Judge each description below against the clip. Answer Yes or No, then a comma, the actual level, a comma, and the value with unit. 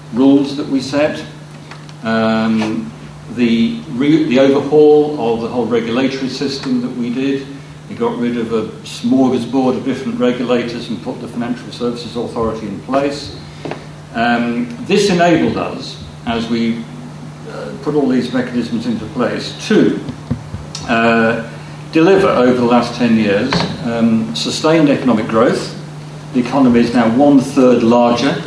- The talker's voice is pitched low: Yes, low, 125 Hz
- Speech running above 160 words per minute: No, average, 140 wpm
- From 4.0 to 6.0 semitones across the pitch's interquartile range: No, average, 3.5 semitones